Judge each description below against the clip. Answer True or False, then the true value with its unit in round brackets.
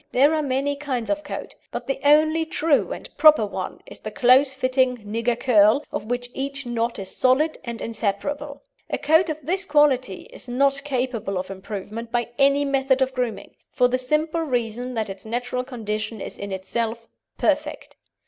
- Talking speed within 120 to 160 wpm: False (175 wpm)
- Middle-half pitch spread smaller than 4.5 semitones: True (3.8 semitones)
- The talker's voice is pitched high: True (255 Hz)